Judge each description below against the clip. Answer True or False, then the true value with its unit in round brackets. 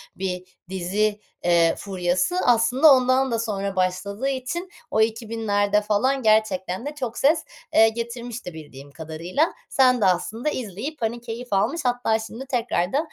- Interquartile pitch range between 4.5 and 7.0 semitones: True (4.9 semitones)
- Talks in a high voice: True (220 Hz)